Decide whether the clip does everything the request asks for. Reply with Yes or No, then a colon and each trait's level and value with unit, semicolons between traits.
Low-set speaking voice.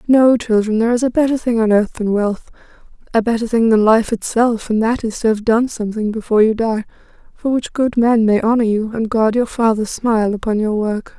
No: high, 225 Hz